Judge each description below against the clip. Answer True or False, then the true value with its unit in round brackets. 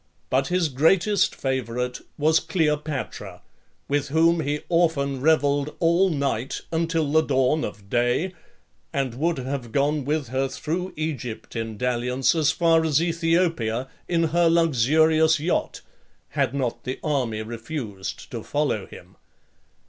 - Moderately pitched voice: True (145 Hz)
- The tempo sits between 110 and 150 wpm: True (135 wpm)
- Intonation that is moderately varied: True (4.3 semitones)